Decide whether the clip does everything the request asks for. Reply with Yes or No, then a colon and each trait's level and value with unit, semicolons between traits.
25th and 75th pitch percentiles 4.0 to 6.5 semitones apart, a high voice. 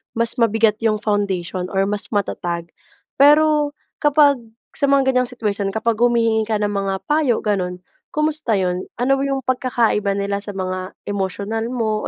Yes: average, 4.4 semitones; high, 220 Hz